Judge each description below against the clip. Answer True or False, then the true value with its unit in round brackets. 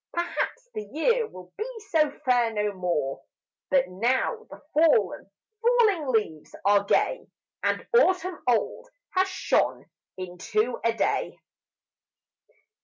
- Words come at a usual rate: False (115 wpm)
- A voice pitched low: False (255 Hz)